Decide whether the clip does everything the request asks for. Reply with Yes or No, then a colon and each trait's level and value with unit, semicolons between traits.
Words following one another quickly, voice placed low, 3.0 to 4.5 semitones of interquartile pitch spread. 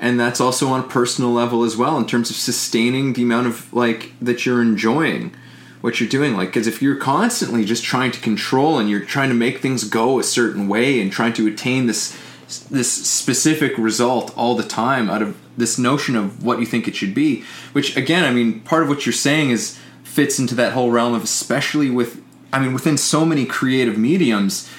No: fast, 215 wpm; low, 120 Hz; narrow, 2.5 semitones